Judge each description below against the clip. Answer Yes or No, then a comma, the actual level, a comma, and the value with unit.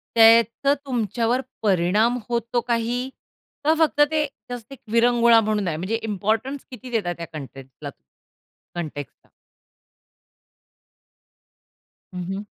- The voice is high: Yes, high, 225 Hz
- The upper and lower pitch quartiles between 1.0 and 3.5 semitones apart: No, average, 4.1 semitones